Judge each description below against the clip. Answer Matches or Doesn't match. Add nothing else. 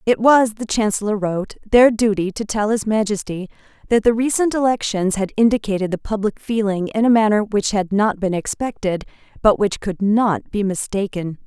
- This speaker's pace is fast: Doesn't match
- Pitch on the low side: Doesn't match